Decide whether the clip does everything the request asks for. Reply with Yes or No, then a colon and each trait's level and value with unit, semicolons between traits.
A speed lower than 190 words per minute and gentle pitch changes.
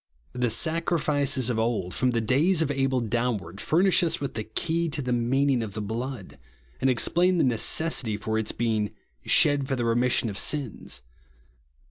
No: average, 170 wpm; average, 4.5 semitones